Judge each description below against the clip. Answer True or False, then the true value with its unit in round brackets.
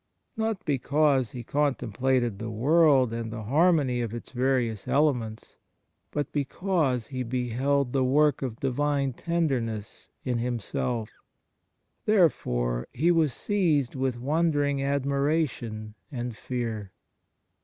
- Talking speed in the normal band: False (110 wpm)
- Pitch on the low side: True (130 Hz)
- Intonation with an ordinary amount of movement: True (3.8 semitones)